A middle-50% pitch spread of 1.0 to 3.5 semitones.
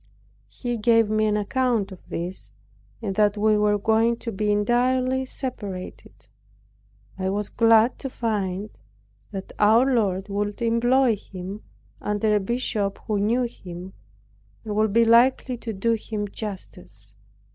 Yes: average, 2.7 semitones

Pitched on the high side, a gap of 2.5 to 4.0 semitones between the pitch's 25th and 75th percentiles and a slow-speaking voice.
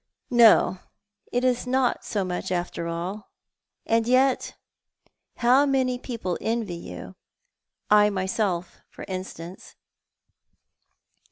No: high, 215 Hz; average, 5.3 semitones; slow, 105 wpm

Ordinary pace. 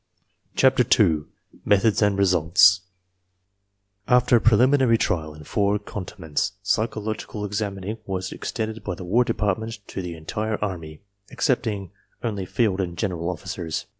No: slow, 130 wpm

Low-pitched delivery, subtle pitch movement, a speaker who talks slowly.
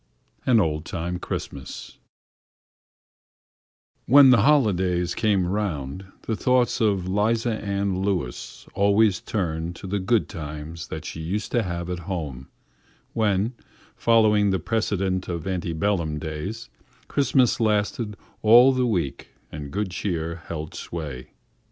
No: very low, 95 Hz; average, 4.5 semitones; slow, 125 wpm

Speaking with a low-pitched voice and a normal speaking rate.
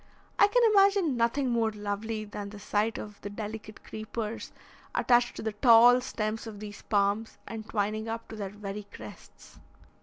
No: high, 220 Hz; average, 170 wpm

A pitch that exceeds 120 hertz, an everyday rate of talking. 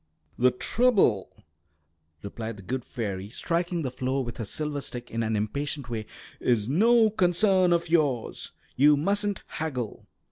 Yes: low, 135 Hz; average, 145 wpm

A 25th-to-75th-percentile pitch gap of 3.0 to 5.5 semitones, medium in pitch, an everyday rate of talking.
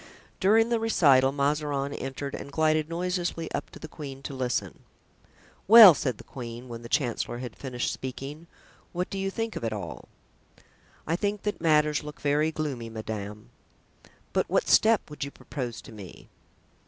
Yes: average, 4.9 semitones; medium, 145 Hz; average, 165 wpm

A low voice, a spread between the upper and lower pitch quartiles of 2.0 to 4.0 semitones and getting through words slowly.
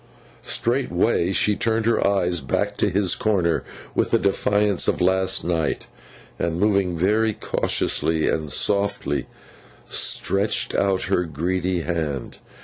Yes: very low, 95 Hz; average, 3.2 semitones; slow, 125 wpm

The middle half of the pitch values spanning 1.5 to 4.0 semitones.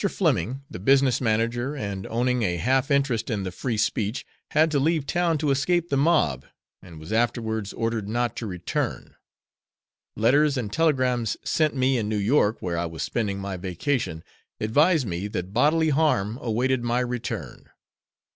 No: average, 5.2 semitones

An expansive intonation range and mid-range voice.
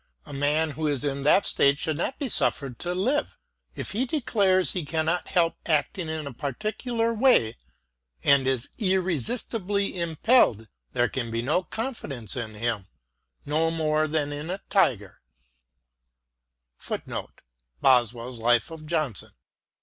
Yes: wide, 5.8 semitones; medium, 160 Hz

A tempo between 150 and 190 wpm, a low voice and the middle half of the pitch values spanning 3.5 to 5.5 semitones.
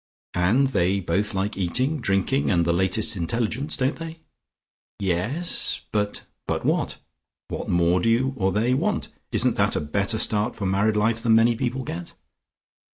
Yes: average, 165 wpm; low, 105 Hz; average, 4.6 semitones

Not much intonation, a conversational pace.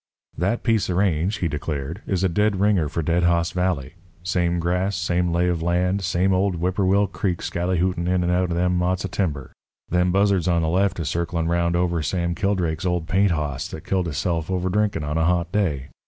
No: narrow, 1.9 semitones; fast, 210 wpm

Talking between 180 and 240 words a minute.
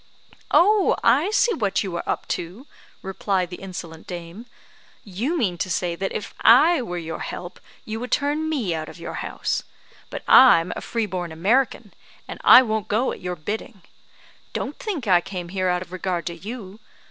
Yes: average, 185 wpm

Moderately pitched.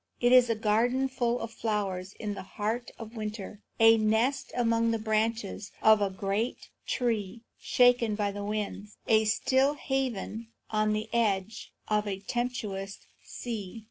No: high, 220 Hz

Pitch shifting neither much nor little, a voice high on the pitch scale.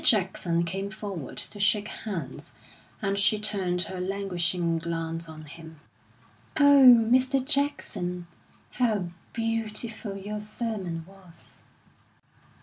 Yes: average, 4.2 semitones; high, 195 Hz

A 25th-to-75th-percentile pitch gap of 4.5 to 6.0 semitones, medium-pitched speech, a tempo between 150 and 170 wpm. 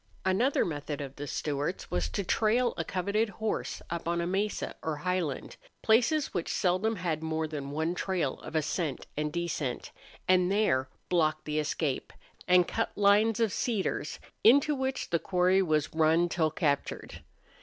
Yes: average, 4.8 semitones; medium, 175 Hz; average, 160 wpm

